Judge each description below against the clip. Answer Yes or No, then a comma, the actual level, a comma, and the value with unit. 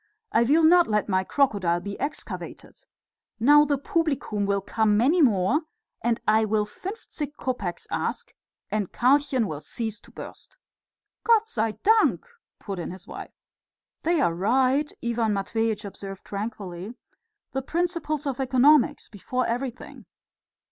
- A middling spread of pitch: No, wide, 6.0 semitones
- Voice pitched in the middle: No, high, 235 Hz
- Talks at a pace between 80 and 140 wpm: Yes, slow, 135 wpm